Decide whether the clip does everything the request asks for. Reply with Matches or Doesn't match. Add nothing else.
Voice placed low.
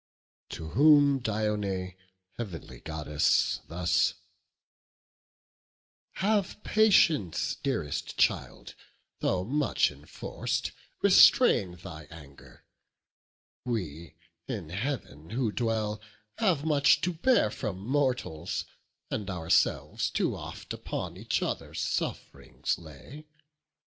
Matches